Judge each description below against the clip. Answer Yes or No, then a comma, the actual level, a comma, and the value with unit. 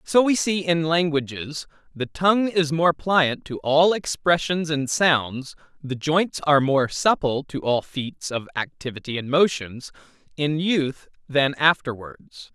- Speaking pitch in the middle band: Yes, medium, 150 Hz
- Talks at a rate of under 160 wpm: Yes, average, 150 wpm